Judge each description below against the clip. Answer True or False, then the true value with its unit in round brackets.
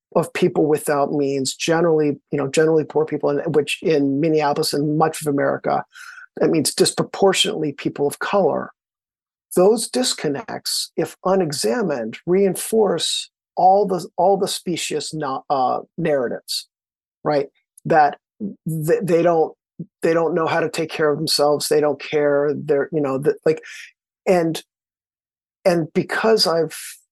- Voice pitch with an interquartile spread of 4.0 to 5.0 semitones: True (4.4 semitones)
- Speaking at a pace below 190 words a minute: True (140 wpm)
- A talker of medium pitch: True (160 Hz)